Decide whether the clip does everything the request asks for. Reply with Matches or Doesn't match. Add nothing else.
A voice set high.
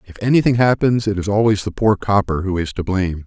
Doesn't match